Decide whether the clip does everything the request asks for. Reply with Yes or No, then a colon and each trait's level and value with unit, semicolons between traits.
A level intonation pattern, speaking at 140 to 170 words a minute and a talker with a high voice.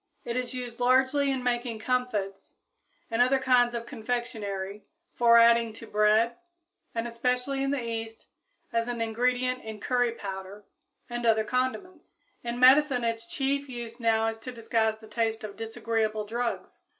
Yes: narrow, 2.0 semitones; average, 155 wpm; high, 235 Hz